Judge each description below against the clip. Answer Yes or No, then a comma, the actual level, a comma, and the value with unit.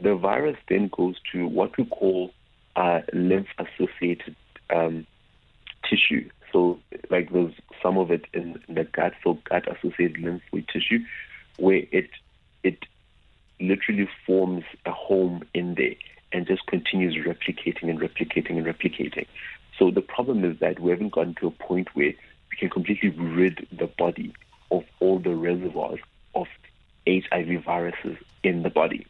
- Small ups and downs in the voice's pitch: Yes, narrow, 1.5 semitones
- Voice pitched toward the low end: Yes, very low, 90 Hz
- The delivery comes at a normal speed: Yes, average, 150 wpm